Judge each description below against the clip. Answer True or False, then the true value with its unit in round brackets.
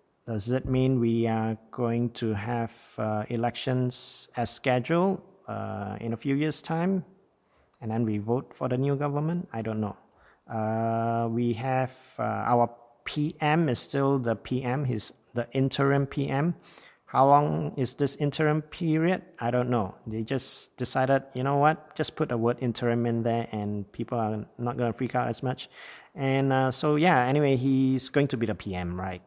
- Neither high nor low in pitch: False (125 Hz)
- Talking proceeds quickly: False (175 wpm)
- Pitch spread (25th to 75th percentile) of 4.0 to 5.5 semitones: False (3.3 semitones)